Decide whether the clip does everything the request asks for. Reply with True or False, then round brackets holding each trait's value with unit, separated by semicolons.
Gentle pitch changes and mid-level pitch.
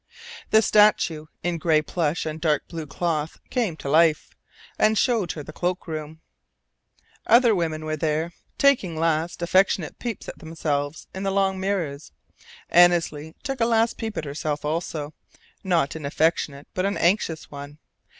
False (3.8 semitones; 165 Hz)